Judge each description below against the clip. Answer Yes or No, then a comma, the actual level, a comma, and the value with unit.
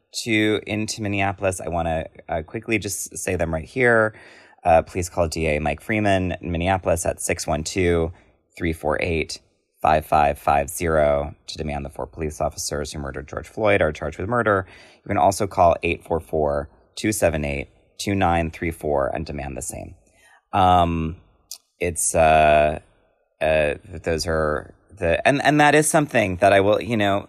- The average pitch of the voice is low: Yes, very low, 85 Hz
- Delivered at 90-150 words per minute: Yes, average, 140 wpm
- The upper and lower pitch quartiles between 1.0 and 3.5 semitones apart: No, average, 4.3 semitones